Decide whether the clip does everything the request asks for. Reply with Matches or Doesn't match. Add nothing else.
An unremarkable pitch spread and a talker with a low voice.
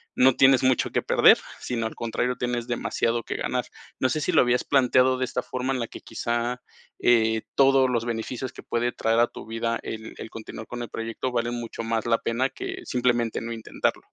Doesn't match